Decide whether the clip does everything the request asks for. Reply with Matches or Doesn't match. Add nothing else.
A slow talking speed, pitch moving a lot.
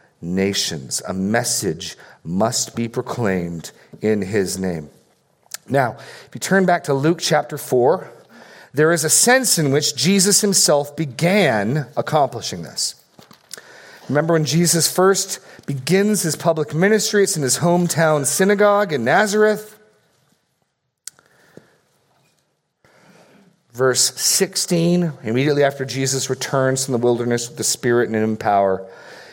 Matches